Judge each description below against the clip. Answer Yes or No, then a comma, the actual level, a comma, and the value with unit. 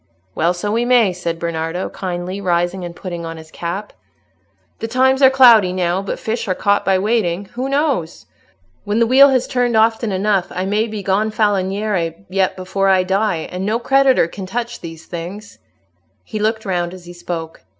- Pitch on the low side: No, high, 195 Hz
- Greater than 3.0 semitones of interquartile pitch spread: Yes, average, 4.2 semitones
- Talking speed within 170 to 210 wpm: Yes, average, 180 wpm